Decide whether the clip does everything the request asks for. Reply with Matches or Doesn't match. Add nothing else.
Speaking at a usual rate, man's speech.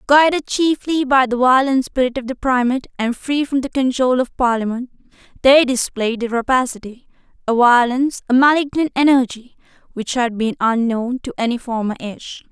Doesn't match